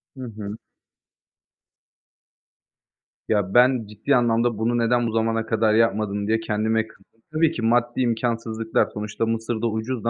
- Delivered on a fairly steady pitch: Yes, narrow, 1.5 semitones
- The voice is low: Yes, low, 115 Hz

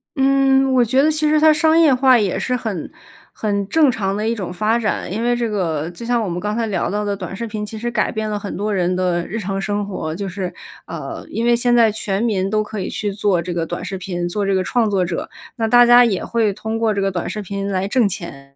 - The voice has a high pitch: Yes, high, 210 Hz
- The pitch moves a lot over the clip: No, average, 3.7 semitones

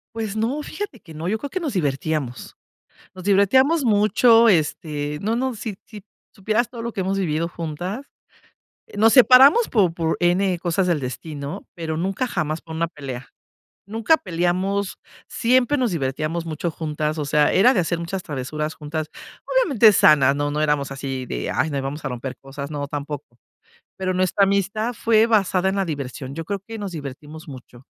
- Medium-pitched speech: Yes, medium, 175 Hz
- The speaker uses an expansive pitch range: Yes, wide, 6.3 semitones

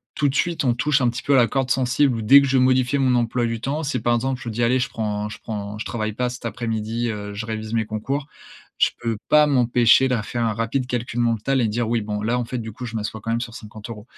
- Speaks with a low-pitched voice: Yes, low, 120 Hz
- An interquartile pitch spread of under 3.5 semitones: Yes, average, 2.7 semitones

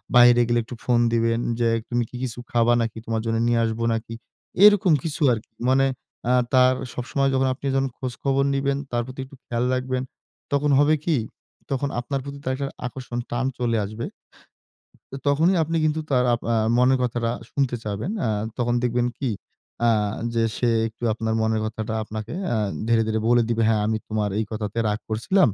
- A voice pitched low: Yes, low, 120 Hz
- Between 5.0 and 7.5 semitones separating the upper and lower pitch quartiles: No, average, 2.9 semitones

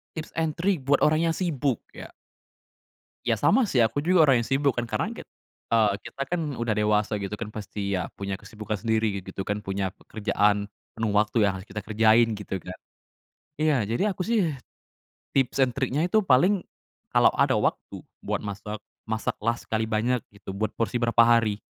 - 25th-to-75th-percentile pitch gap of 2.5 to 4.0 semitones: No, average, 4.8 semitones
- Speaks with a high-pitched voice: No, low, 115 Hz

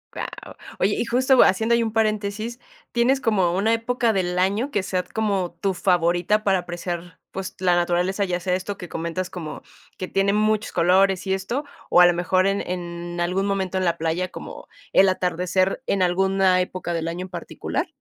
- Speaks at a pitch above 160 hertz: Yes, medium, 185 Hz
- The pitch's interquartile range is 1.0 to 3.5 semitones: Yes, narrow, 2.5 semitones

